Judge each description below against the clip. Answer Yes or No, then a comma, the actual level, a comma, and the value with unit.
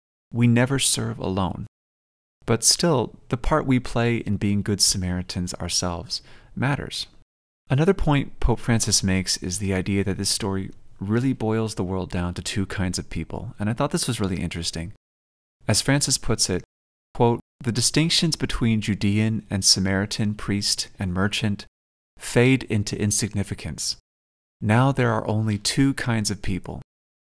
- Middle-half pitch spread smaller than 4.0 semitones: No, average, 4.3 semitones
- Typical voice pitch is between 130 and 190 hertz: No, low, 105 Hz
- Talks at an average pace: Yes, average, 150 wpm